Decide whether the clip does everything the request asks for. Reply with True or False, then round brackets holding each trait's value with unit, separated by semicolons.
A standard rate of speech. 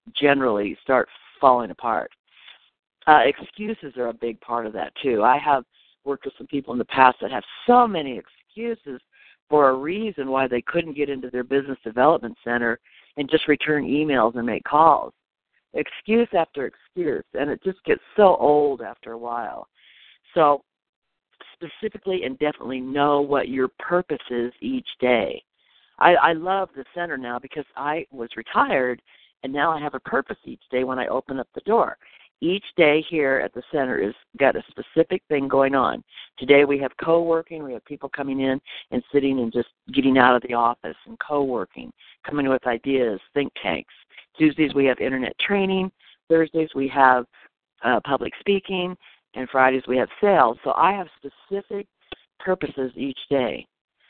True (170 wpm)